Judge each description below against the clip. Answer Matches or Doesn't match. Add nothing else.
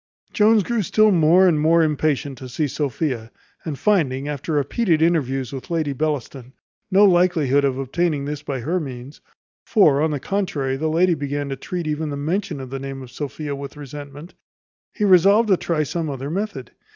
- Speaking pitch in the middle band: Matches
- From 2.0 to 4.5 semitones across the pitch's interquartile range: Matches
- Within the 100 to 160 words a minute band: Doesn't match